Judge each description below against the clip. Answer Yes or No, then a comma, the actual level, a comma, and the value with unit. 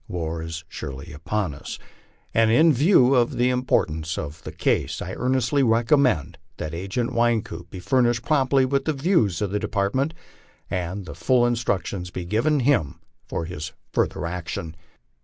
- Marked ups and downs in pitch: Yes, wide, 7.2 semitones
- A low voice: Yes, low, 110 Hz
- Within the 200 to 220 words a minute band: No, average, 160 wpm